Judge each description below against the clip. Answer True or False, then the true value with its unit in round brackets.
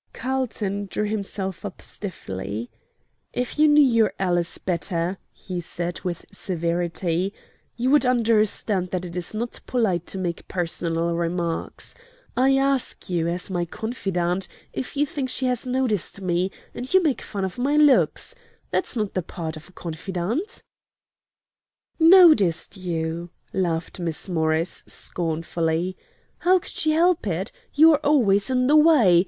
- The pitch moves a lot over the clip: True (6.7 semitones)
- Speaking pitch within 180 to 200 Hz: True (190 Hz)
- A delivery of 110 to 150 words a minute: True (145 wpm)